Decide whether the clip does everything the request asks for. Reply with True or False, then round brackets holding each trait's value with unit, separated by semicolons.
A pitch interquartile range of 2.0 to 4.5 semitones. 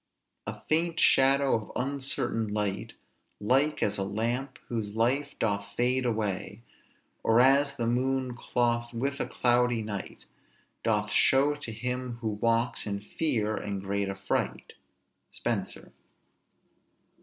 True (4.0 semitones)